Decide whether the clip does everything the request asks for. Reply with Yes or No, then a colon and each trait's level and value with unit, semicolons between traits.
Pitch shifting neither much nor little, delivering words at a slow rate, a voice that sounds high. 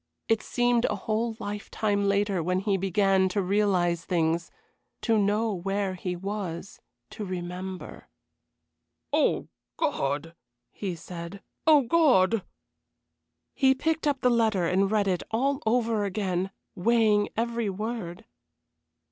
Yes: average, 3.6 semitones; slow, 120 wpm; high, 200 Hz